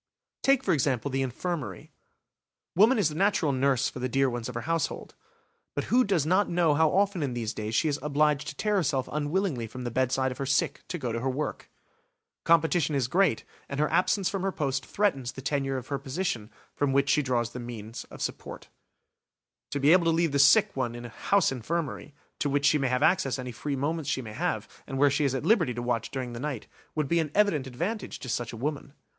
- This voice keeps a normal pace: No, fast, 230 wpm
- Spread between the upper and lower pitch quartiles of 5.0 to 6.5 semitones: No, average, 4.5 semitones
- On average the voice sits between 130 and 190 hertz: Yes, medium, 140 Hz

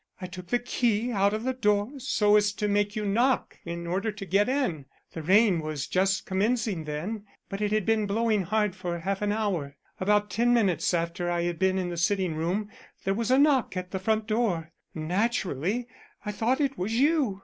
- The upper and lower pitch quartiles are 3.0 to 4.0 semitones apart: Yes, average, 3.7 semitones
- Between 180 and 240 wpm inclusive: Yes, fast, 205 wpm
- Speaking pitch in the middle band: No, high, 205 Hz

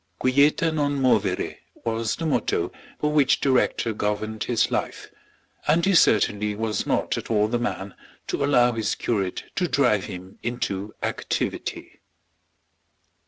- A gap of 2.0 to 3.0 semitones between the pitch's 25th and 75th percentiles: No, average, 5.2 semitones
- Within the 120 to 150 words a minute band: Yes, average, 140 wpm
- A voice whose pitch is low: Yes, low, 115 Hz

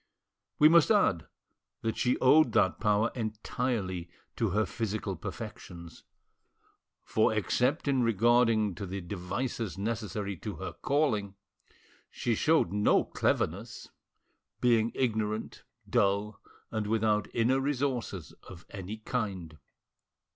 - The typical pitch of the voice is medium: No, low, 110 Hz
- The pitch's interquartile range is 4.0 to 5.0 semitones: No, average, 3.6 semitones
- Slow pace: Yes, slow, 110 wpm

